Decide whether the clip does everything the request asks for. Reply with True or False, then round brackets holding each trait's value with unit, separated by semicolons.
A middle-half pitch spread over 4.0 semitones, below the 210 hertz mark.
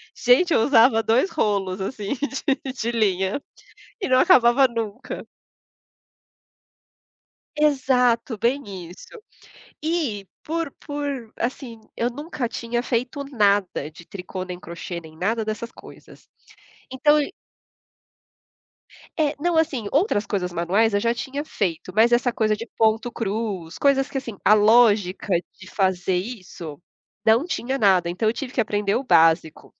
False (5.1 semitones; 230 Hz)